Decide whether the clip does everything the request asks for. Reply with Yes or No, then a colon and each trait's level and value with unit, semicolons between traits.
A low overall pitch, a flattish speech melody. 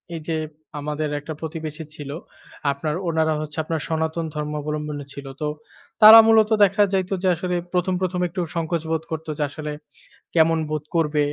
No: medium, 160 Hz; narrow, 2.0 semitones